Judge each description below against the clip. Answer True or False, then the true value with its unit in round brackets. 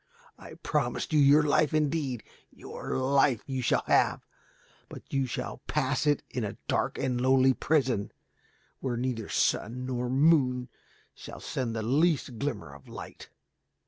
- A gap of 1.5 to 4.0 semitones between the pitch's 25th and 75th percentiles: True (2.7 semitones)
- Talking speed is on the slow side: False (145 wpm)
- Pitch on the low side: True (130 Hz)